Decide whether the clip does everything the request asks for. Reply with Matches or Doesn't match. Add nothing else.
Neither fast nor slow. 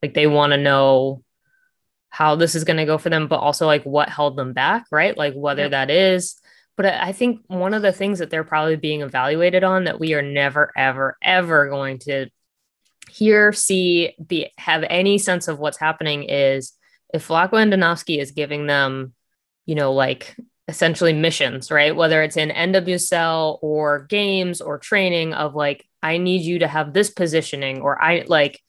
Matches